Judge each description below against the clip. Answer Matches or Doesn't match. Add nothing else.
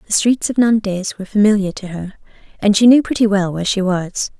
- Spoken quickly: Matches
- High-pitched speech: Matches